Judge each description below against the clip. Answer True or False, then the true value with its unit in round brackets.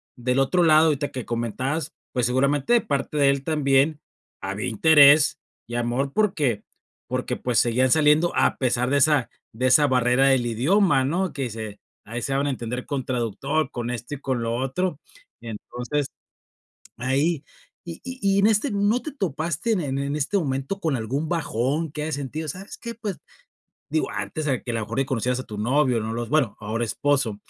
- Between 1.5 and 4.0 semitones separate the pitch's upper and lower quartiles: False (4.4 semitones)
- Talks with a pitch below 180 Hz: True (135 Hz)